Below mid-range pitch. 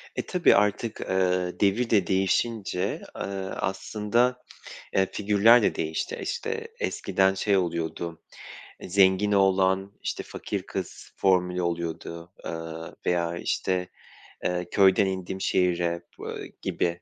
Yes: very low, 95 Hz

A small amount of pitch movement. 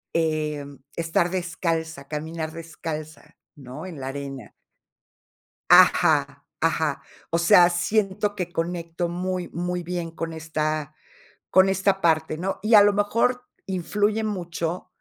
No: average, 3.0 semitones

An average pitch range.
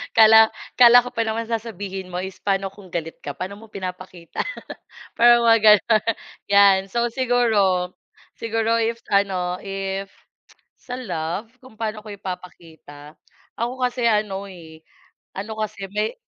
Yes: average, 3.5 semitones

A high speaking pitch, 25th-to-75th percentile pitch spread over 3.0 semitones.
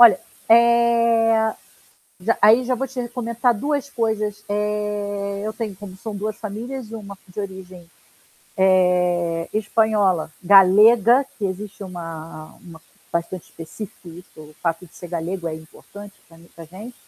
Yes: high, 205 Hz; average, 3.9 semitones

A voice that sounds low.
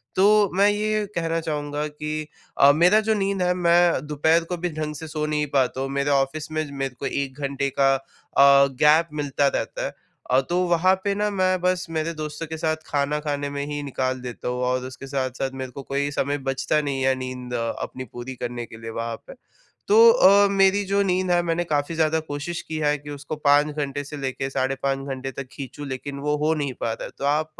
No: medium, 150 Hz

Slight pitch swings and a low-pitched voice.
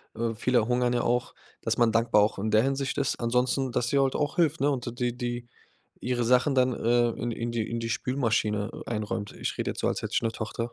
Yes: narrow, 1.8 semitones; low, 120 Hz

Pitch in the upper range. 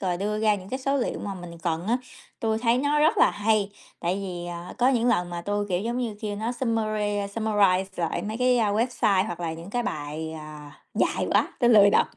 Yes: high, 205 Hz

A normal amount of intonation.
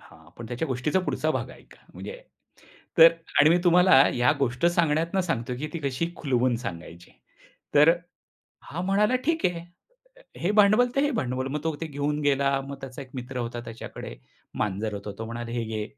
No: wide, 6.0 semitones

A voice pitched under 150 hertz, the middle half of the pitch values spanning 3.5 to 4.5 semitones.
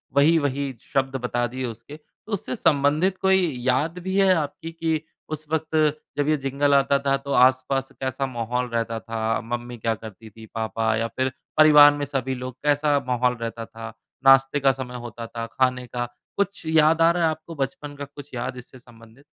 Yes: low, 135 Hz; average, 3.8 semitones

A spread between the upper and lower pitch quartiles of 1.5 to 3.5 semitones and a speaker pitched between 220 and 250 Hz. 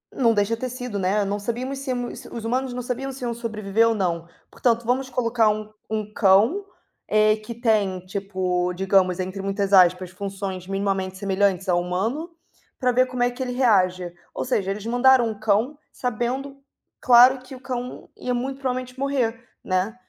No: average, 4.3 semitones; high, 225 Hz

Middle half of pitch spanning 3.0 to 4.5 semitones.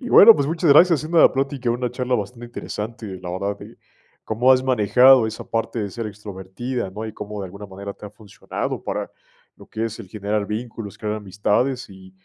Yes: average, 3.8 semitones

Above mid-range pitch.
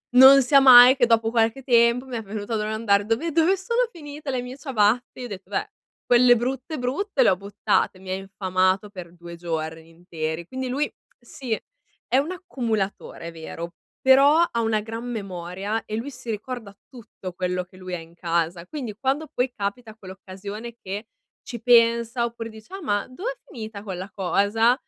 Yes: high, 225 Hz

